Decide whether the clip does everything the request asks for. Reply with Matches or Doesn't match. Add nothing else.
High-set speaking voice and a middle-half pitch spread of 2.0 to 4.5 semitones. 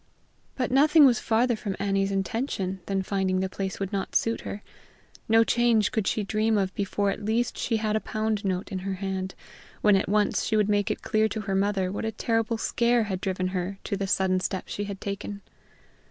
Matches